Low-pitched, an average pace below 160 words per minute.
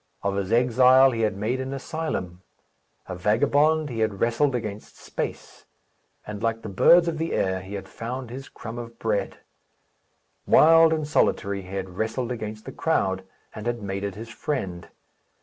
No: low, 115 Hz; average, 170 wpm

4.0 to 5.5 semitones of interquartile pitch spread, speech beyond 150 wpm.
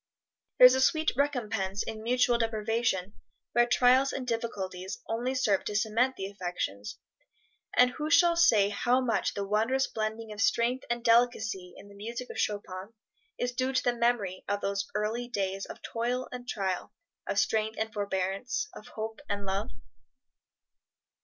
No: average, 3.6 semitones; average, 160 wpm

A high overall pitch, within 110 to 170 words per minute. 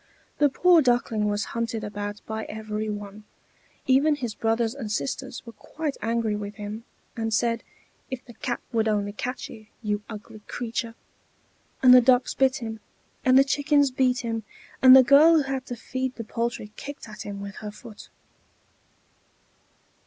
Yes: high, 230 Hz; average, 165 wpm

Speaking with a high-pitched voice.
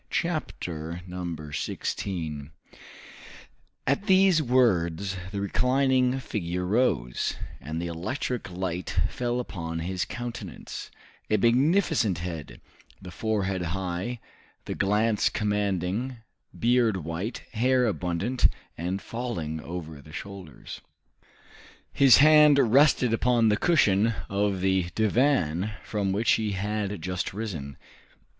No: low, 100 Hz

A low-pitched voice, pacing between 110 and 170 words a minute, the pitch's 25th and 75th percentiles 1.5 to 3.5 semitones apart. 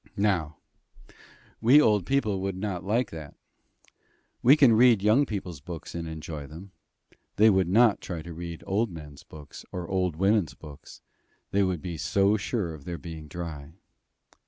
No: very low, 90 Hz; average, 160 wpm; average, 4.6 semitones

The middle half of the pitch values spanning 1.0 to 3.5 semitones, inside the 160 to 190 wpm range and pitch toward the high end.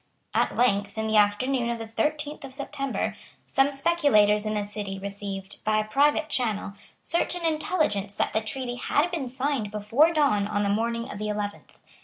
No: average, 5.3 semitones; average, 180 wpm; high, 225 Hz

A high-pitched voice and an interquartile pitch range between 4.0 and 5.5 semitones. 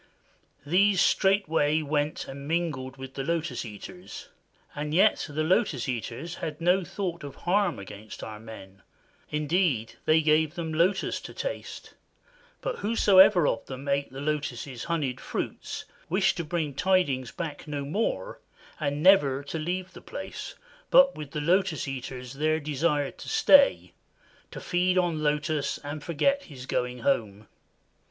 No: medium, 155 Hz; average, 4.6 semitones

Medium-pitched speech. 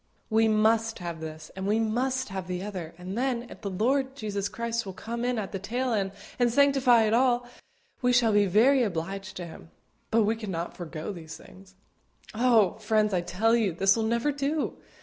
No: high, 220 Hz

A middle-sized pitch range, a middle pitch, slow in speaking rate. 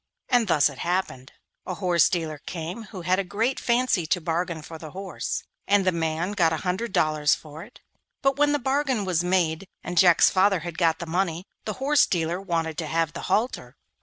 No: average, 3.5 semitones; medium, 175 Hz; fast, 205 wpm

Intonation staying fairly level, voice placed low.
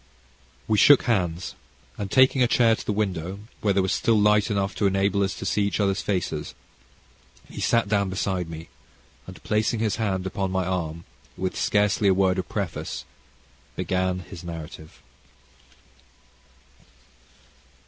Yes: narrow, 2.3 semitones; very low, 95 Hz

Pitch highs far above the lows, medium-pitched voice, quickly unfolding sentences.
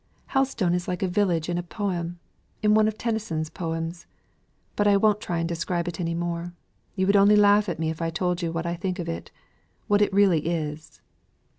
No: average, 3.4 semitones; medium, 175 Hz; fast, 210 wpm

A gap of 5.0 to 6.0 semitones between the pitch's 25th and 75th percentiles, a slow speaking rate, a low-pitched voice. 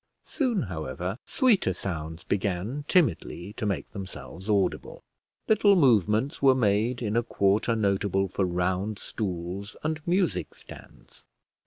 Yes: wide, 5.6 semitones; slow, 125 wpm; low, 105 Hz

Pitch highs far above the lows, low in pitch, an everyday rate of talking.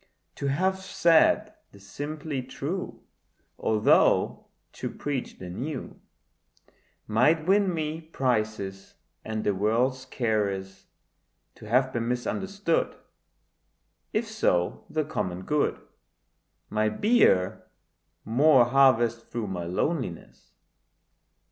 No: wide, 6.5 semitones; low, 130 Hz; slow, 100 wpm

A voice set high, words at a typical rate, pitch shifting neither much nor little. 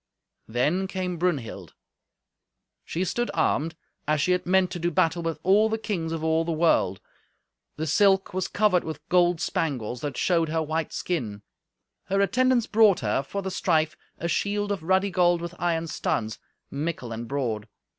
No: medium, 170 Hz; average, 170 wpm; average, 3.7 semitones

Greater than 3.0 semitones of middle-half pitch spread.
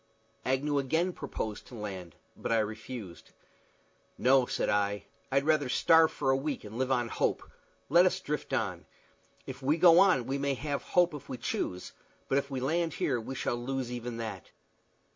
Yes: average, 4.3 semitones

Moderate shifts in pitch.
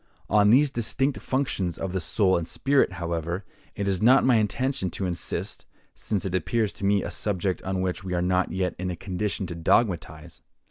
Yes: average, 3.2 semitones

